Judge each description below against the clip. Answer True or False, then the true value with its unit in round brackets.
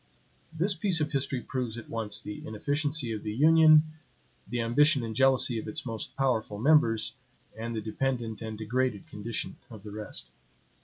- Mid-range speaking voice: False (120 Hz)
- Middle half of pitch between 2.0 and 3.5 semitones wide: False (4.5 semitones)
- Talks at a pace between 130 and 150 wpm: False (165 wpm)